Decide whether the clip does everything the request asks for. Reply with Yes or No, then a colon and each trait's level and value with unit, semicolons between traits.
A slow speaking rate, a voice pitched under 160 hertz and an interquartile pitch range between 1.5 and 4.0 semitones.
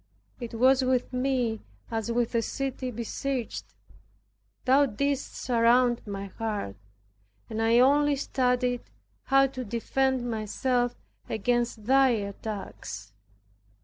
No: slow, 110 wpm; high, 245 Hz; average, 2.8 semitones